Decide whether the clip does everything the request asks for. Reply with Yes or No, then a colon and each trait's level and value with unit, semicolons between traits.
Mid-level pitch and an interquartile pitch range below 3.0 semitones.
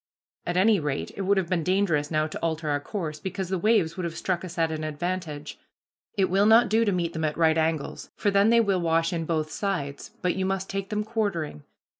No: medium, 175 Hz; average, 3.8 semitones